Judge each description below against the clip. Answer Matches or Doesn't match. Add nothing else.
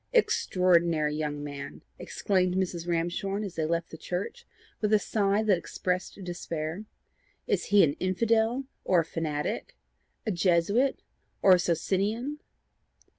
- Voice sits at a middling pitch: Matches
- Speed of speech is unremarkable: Doesn't match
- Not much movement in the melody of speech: Doesn't match